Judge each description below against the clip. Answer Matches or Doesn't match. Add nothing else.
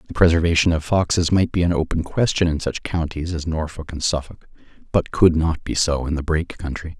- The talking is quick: Matches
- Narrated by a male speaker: Matches